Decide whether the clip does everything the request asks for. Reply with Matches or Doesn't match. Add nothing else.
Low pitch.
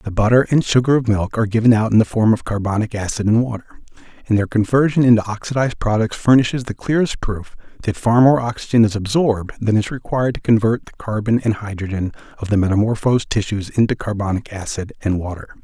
Matches